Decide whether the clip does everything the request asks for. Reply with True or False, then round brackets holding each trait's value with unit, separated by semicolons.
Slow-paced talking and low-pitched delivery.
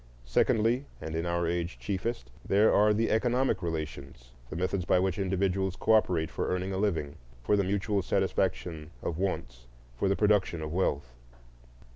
False (155 wpm; 95 Hz)